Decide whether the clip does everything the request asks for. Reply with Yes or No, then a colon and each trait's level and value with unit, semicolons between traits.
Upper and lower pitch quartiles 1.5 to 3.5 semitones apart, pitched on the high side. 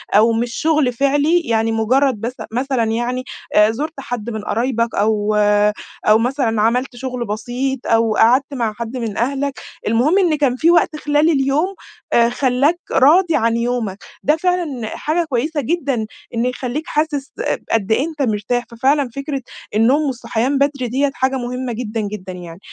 No: average, 3.9 semitones; very high, 250 Hz